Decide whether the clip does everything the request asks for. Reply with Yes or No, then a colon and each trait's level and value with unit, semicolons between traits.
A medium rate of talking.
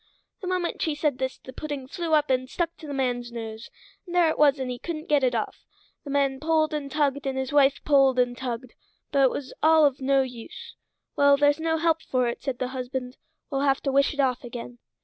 No: fast, 235 wpm